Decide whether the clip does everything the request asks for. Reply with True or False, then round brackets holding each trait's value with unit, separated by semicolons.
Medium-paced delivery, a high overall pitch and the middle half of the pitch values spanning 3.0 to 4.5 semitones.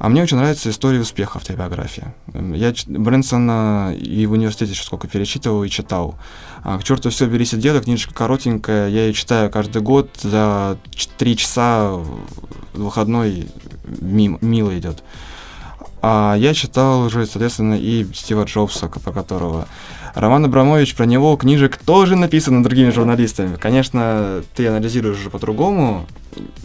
False (140 wpm; 110 Hz; 3.9 semitones)